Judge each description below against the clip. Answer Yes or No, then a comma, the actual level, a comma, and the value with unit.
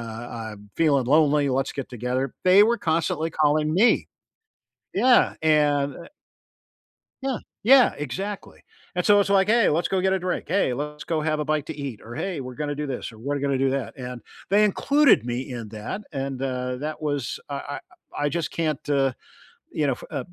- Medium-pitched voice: Yes, medium, 145 Hz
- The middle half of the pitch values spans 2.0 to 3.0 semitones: No, average, 4.9 semitones